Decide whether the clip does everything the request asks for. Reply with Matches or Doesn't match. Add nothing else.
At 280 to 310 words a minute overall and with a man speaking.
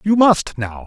Doesn't match